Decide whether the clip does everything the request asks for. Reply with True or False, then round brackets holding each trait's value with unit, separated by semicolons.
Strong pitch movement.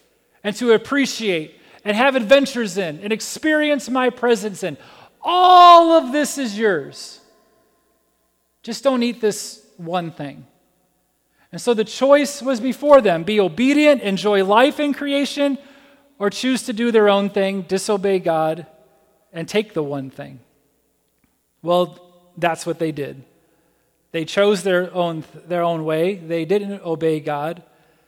True (7.1 semitones)